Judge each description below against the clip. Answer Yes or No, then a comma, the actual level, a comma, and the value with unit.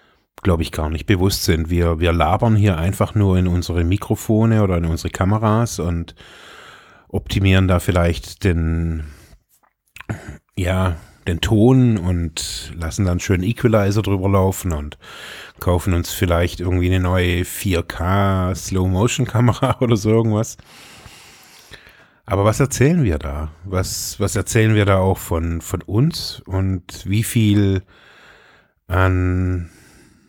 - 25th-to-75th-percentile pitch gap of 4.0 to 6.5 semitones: No, average, 3.5 semitones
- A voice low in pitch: Yes, very low, 95 Hz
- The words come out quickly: No, slow, 125 wpm